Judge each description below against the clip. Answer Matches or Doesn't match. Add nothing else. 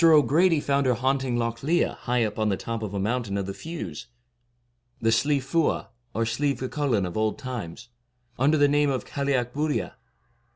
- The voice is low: Matches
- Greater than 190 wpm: Matches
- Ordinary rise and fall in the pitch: Matches